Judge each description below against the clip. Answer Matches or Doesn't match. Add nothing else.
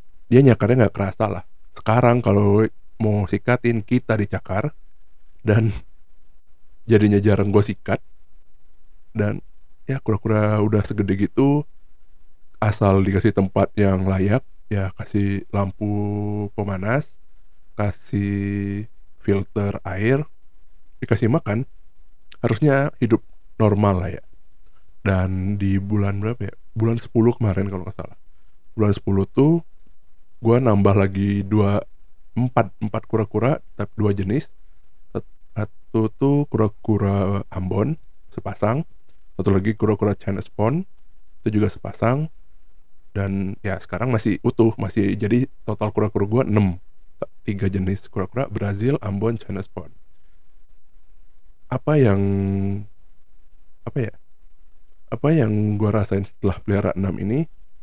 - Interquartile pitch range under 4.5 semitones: Matches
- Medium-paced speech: Matches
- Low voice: Matches